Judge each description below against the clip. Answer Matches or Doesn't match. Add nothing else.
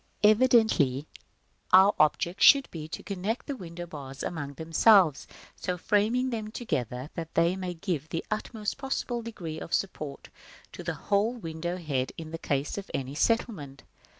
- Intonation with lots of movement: Matches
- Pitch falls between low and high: Matches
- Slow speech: Doesn't match